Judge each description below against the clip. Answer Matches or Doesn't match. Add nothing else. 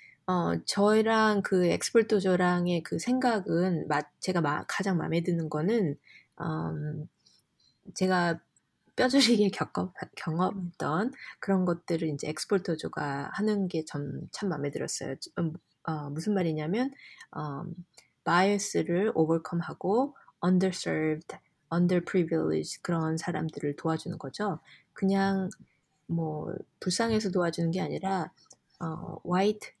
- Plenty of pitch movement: Doesn't match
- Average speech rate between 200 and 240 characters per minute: Doesn't match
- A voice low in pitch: Doesn't match